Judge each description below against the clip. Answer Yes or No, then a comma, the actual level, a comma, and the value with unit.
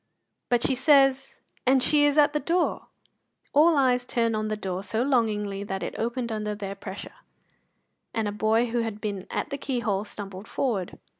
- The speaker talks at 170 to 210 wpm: Yes, average, 180 wpm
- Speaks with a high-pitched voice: Yes, high, 230 Hz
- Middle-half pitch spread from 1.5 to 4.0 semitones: No, average, 4.4 semitones